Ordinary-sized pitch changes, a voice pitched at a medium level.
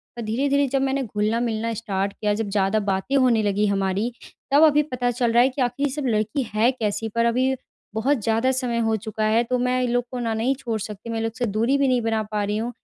No: average, 3.0 semitones; high, 230 Hz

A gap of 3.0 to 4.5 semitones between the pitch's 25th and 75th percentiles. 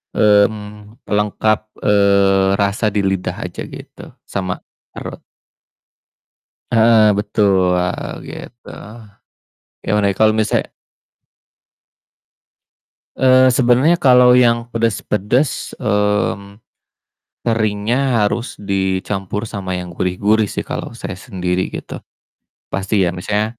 No: narrow, 2.4 semitones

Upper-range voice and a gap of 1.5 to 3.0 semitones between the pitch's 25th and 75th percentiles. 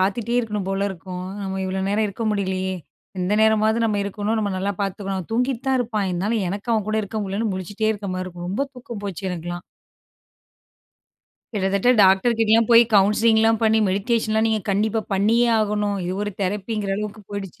Yes: high, 205 Hz; narrow, 2.4 semitones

